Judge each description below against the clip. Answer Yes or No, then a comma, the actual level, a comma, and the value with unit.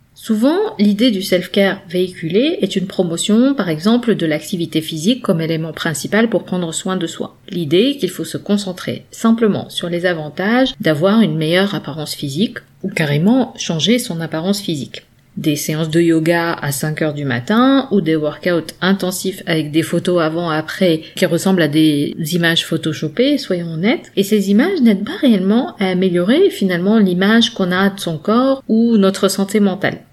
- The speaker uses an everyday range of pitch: Yes, average, 4.6 semitones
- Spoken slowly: No, average, 170 wpm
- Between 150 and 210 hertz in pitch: Yes, medium, 185 Hz